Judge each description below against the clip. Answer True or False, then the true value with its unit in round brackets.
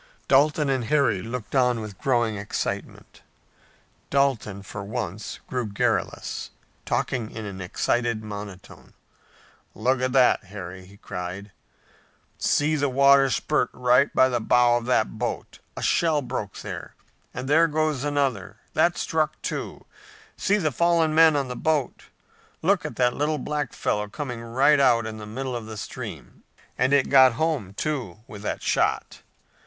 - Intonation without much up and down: False (4.7 semitones)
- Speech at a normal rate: True (155 wpm)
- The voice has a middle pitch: False (125 Hz)